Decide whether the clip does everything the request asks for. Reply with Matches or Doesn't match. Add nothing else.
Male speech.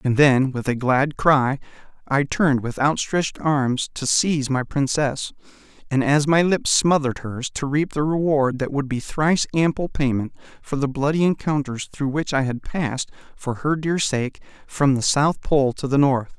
Matches